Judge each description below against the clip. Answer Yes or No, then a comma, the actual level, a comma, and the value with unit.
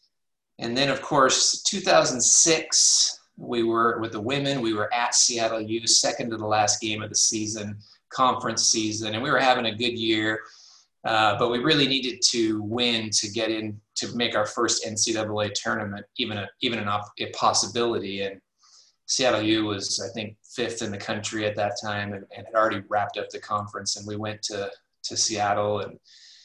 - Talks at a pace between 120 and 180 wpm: No, average, 190 wpm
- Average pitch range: No, narrow, 2.0 semitones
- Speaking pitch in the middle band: No, low, 110 Hz